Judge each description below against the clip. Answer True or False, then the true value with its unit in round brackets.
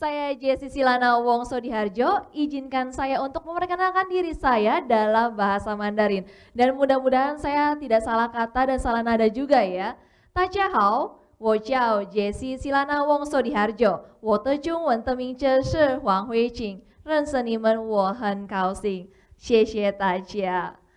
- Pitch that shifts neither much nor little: True (4.5 semitones)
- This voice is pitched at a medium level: False (245 Hz)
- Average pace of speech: False (150 wpm)